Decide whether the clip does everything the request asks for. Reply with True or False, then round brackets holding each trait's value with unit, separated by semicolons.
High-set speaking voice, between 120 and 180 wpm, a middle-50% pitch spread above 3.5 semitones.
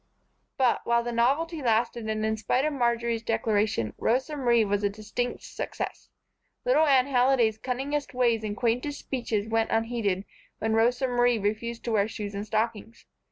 False (235 Hz; 160 wpm; 2.4 semitones)